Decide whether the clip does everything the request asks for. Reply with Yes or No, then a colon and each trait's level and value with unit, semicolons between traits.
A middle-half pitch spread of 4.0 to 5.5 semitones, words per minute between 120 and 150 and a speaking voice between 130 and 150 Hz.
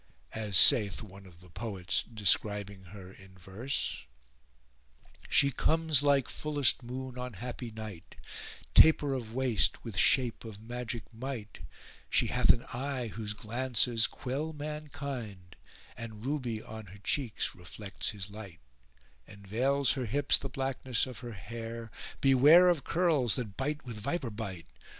No: average, 4.5 semitones; average, 145 wpm; low, 115 Hz